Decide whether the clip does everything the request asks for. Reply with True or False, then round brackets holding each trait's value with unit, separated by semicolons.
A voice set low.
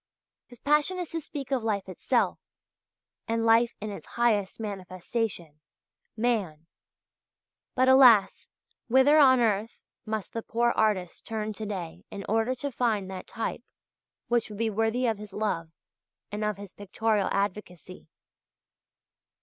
False (220 Hz)